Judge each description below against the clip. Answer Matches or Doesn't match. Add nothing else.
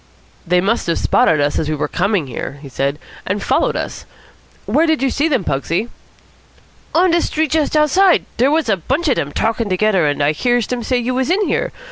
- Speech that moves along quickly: Matches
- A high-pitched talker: Matches